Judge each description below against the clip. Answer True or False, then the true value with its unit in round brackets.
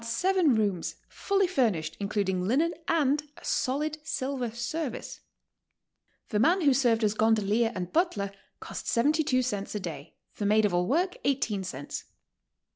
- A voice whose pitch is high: True (235 Hz)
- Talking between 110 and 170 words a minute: True (150 wpm)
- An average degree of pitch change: False (6.7 semitones)